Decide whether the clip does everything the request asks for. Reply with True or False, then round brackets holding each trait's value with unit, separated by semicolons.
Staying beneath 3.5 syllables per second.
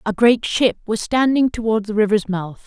False (4.9 syllables/s)